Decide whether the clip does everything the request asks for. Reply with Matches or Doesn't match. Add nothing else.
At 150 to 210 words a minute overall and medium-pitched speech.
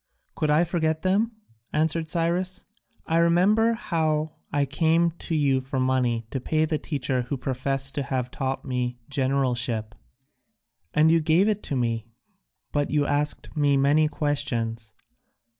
Doesn't match